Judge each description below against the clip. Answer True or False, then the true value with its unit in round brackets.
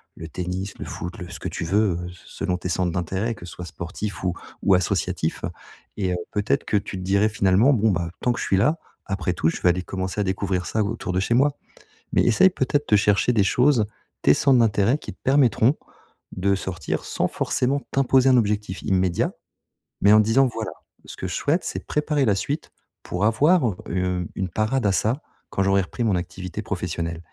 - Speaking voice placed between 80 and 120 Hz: True (100 Hz)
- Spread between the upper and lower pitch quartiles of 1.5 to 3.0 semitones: False (4.1 semitones)